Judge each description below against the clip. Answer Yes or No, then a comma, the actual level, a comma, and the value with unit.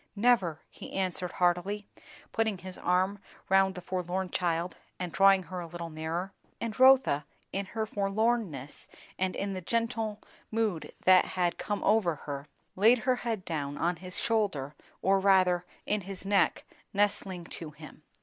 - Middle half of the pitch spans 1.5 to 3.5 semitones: Yes, average, 3.0 semitones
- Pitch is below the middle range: No, medium, 185 Hz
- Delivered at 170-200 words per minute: No, average, 155 wpm